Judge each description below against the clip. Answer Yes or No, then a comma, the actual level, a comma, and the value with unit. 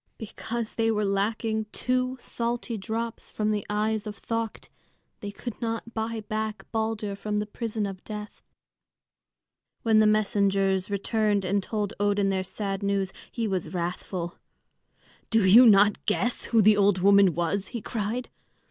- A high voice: Yes, high, 210 Hz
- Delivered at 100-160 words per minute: Yes, average, 150 wpm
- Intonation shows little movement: Yes, narrow, 2.1 semitones